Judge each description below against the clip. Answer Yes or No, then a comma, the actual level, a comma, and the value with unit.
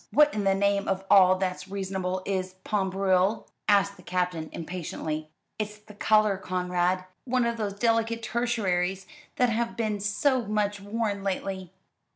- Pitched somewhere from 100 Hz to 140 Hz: No, high, 200 Hz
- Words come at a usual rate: Yes, average, 155 wpm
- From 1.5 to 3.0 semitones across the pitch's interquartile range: Yes, narrow, 2.6 semitones